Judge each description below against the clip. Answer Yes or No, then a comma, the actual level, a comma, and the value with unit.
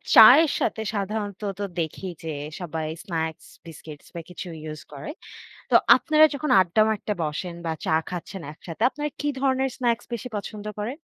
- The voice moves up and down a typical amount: No, wide, 6.7 semitones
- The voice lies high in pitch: Yes, high, 200 Hz